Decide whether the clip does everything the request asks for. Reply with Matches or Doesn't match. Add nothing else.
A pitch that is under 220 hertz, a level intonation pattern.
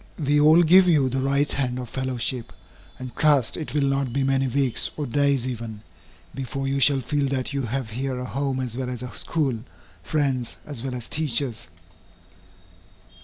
Matches